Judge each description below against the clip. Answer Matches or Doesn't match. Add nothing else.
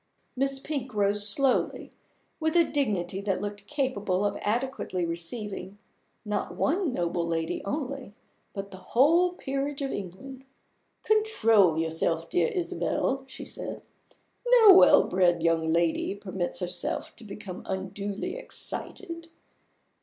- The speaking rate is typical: Doesn't match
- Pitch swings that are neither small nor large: Doesn't match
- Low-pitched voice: Doesn't match